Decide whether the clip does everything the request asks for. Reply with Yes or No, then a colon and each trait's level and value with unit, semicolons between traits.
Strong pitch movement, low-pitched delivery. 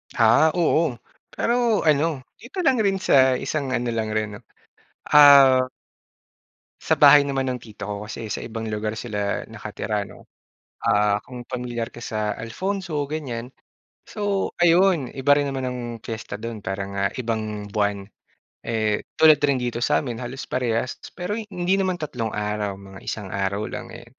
Yes: wide, 5.8 semitones; low, 125 Hz